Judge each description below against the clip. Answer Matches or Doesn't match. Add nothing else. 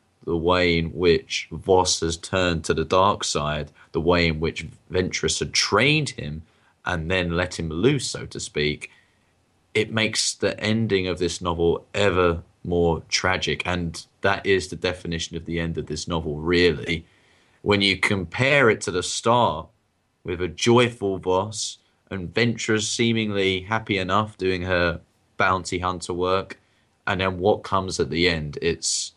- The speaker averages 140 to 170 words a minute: Matches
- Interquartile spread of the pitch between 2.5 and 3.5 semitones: Matches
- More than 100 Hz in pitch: Doesn't match